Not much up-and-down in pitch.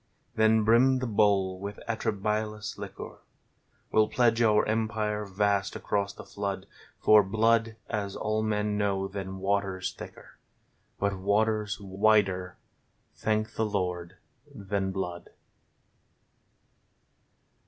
Yes: narrow, 1.9 semitones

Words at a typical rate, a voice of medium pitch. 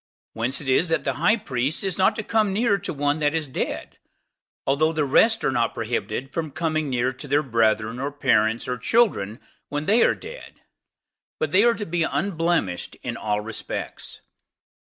Yes: average, 185 wpm; medium, 145 Hz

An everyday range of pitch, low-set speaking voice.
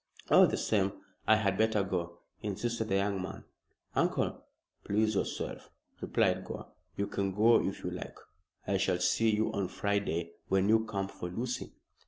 No: narrow, 2.3 semitones; low, 100 Hz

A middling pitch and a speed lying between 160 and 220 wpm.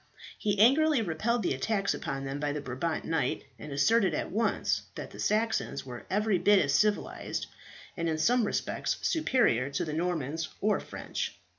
Yes: medium, 175 Hz; average, 170 wpm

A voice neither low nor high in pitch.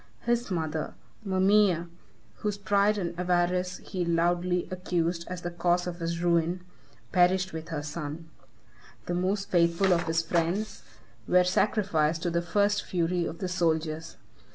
Yes: medium, 175 Hz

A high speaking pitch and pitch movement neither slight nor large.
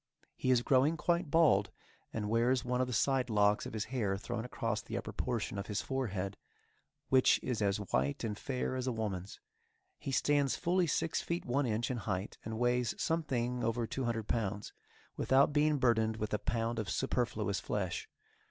No: low, 120 Hz; average, 3.8 semitones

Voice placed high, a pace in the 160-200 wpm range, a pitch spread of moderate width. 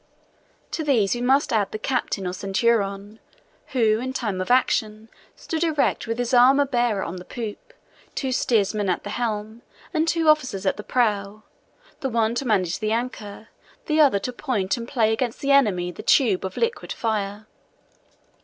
Yes: high, 225 Hz; average, 175 wpm; average, 4.1 semitones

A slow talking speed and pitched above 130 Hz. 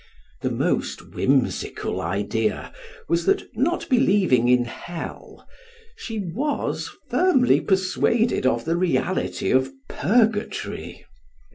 Yes: slow, 100 wpm; medium, 185 Hz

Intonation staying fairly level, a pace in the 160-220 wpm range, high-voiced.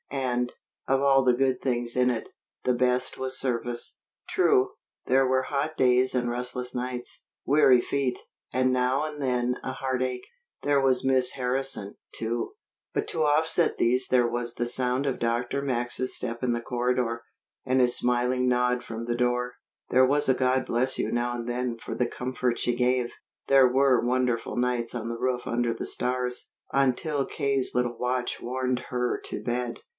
No: narrow, 1.2 semitones; average, 175 wpm; low, 125 Hz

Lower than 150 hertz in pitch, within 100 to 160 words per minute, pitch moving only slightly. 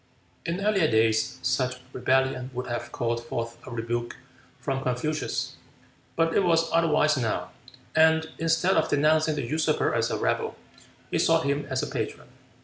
No: medium, 140 Hz; average, 155 wpm; average, 4.8 semitones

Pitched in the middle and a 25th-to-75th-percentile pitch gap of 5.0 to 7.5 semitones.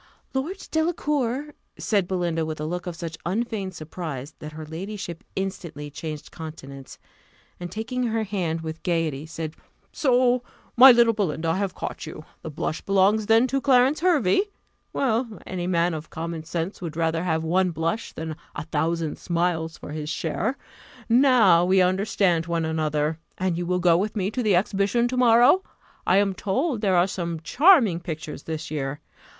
Yes: medium, 180 Hz; wide, 5.6 semitones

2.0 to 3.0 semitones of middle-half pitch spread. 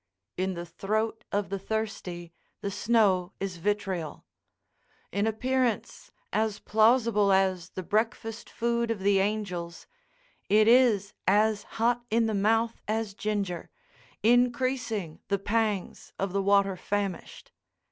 Yes: narrow, 2.6 semitones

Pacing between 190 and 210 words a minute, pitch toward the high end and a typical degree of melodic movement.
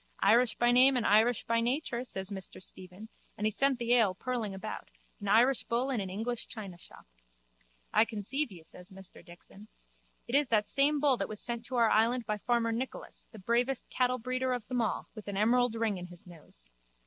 Yes: average, 200 wpm; high, 230 Hz; average, 3.5 semitones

